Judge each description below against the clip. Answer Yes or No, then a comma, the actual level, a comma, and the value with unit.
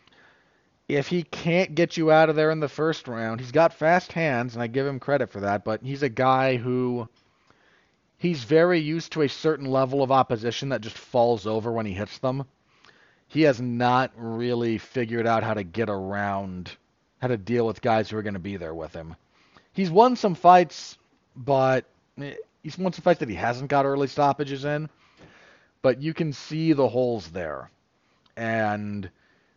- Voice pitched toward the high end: No, low, 130 Hz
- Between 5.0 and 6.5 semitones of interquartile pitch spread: Yes, wide, 5.5 semitones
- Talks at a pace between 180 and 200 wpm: Yes, average, 185 wpm